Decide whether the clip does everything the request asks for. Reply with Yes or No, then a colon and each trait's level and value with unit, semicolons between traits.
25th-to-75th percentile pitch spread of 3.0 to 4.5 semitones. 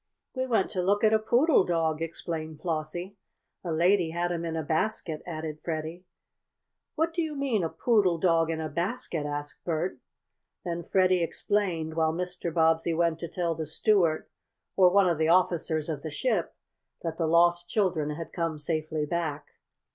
No: narrow, 2.6 semitones